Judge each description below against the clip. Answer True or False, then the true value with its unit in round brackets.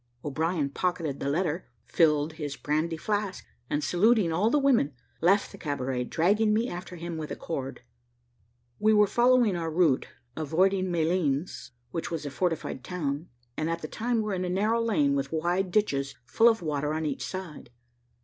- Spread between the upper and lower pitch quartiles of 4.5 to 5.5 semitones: True (4.8 semitones)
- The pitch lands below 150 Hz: False (170 Hz)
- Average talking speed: True (175 wpm)